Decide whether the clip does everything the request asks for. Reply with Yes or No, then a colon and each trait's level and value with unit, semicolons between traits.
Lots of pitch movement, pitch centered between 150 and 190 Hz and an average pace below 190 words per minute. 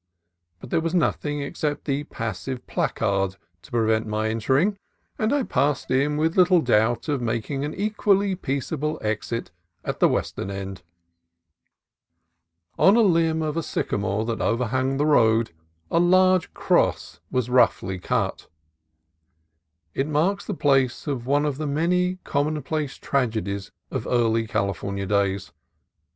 No: wide, 6.2 semitones; low, 135 Hz; average, 140 wpm